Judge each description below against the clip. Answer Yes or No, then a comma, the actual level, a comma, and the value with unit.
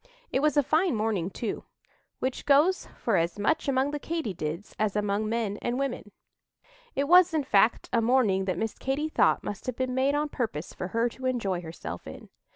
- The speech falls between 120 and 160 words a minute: No, average, 200 wpm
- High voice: Yes, high, 235 Hz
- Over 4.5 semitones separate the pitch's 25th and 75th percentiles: Yes, wide, 5.6 semitones